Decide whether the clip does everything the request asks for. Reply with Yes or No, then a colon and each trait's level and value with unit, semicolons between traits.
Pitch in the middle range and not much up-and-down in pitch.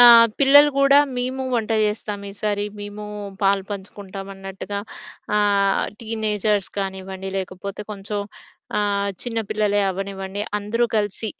No: high, 205 Hz; narrow, 1.8 semitones